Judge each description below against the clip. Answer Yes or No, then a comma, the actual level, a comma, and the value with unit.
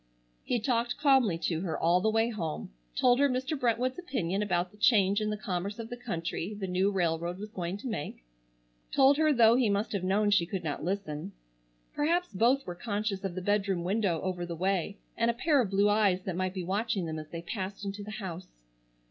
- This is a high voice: Yes, high, 200 Hz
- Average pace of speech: No, fast, 215 wpm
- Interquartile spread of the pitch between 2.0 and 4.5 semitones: Yes, average, 4.2 semitones